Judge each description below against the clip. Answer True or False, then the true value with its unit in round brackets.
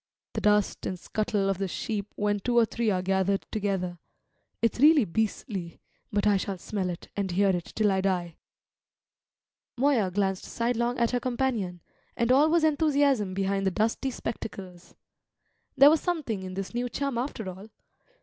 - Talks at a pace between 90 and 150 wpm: False (170 wpm)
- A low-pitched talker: False (210 Hz)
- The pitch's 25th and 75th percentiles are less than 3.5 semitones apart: False (4.2 semitones)